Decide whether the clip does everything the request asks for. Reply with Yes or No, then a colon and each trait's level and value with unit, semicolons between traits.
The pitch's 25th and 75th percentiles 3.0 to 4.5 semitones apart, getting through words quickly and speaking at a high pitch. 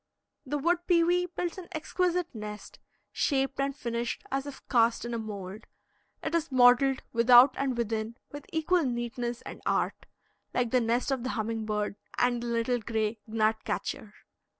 No: average, 3.6 semitones; average, 165 wpm; high, 245 Hz